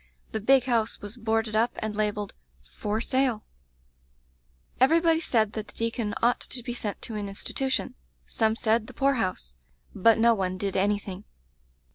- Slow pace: No, average, 160 wpm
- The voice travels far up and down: No, average, 2.7 semitones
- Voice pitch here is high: Yes, high, 220 Hz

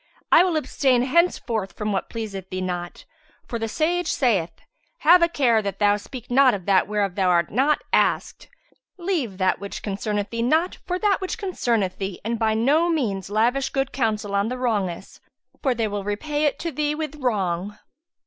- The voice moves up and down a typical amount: No, wide, 6.6 semitones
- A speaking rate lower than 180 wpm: No, average, 185 wpm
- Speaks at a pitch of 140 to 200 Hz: No, high, 230 Hz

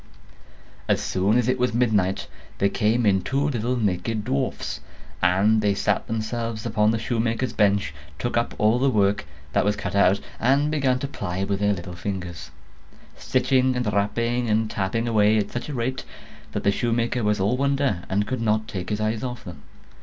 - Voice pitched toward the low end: Yes, low, 110 Hz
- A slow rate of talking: No, average, 185 wpm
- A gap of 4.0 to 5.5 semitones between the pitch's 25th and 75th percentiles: No, average, 3.3 semitones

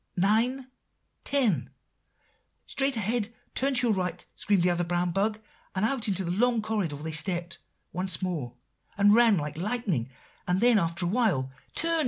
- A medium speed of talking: Yes, average, 160 wpm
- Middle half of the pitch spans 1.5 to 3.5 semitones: No, average, 5.1 semitones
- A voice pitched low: No, high, 195 Hz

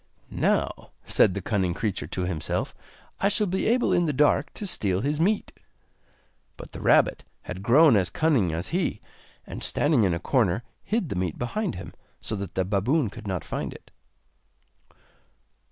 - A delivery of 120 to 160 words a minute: No, average, 170 wpm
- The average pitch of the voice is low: Yes, low, 115 Hz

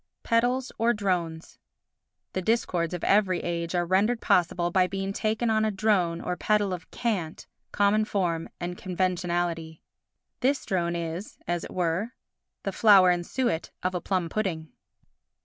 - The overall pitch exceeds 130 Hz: Yes, medium, 185 Hz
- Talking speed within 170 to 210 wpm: No, average, 150 wpm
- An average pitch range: Yes, average, 3.7 semitones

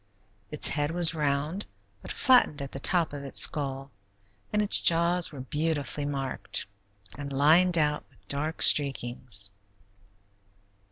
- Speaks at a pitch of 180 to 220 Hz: No, medium, 145 Hz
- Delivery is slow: Yes, slow, 130 wpm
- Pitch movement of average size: Yes, average, 3.2 semitones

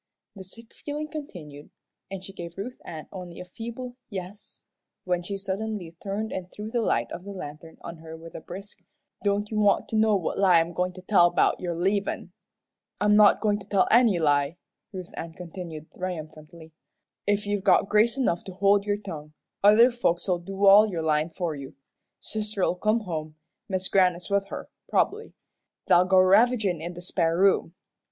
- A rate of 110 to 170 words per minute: No, average, 185 wpm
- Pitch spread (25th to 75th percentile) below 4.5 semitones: Yes, average, 3.4 semitones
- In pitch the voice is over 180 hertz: Yes, high, 190 Hz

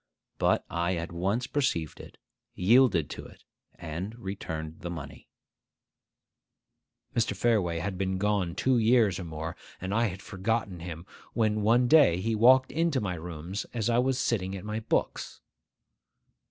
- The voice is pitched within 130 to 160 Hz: No, low, 100 Hz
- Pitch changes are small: No, average, 5.0 semitones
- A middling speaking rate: Yes, average, 155 wpm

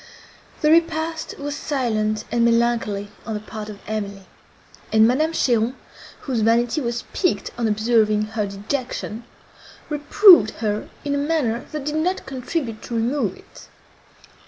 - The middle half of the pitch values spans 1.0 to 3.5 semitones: No, average, 5.2 semitones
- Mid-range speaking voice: No, high, 235 Hz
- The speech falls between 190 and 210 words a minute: No, average, 140 wpm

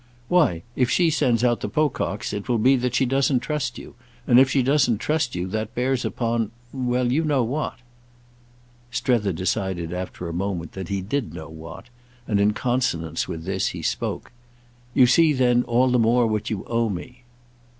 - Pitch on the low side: Yes, low, 120 Hz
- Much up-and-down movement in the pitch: No, average, 4.5 semitones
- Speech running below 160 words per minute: No, average, 180 wpm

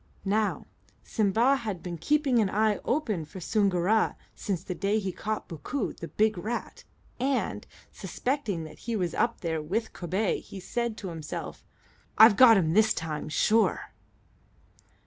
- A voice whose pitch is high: Yes, high, 210 Hz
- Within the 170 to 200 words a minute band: No, average, 150 wpm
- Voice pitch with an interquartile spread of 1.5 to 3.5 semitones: No, average, 4.3 semitones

